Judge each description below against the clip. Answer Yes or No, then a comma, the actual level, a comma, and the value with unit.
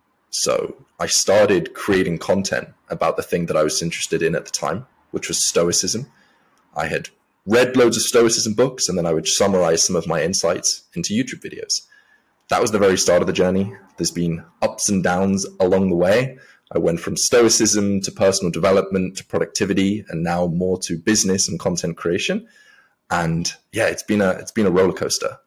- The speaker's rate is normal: Yes, average, 190 wpm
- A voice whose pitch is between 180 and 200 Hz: No, very low, 95 Hz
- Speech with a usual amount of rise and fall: Yes, average, 4.1 semitones